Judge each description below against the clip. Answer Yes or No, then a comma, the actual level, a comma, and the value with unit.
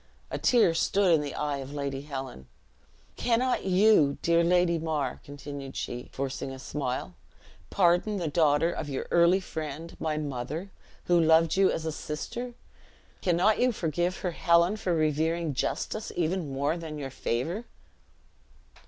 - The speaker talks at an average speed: Yes, average, 150 wpm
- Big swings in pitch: No, average, 3.8 semitones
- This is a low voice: No, medium, 160 Hz